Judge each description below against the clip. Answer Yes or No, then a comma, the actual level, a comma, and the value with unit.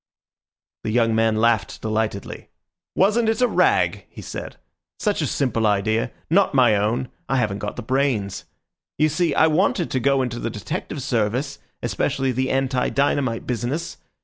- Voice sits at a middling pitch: No, low, 125 Hz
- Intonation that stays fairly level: No, average, 4.3 semitones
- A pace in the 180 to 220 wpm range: No, average, 155 wpm